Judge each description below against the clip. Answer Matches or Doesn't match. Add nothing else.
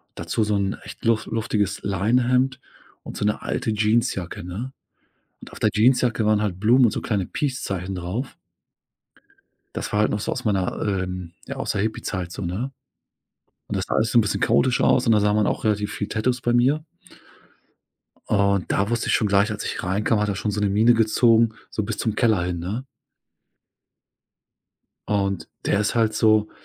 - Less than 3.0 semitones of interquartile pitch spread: Matches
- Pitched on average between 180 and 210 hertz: Doesn't match